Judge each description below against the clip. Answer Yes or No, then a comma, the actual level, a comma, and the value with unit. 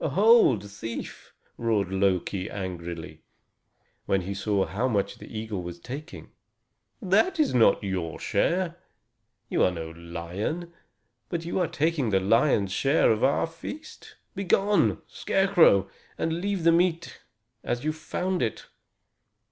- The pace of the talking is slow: Yes, slow, 130 wpm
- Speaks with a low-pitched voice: Yes, low, 115 Hz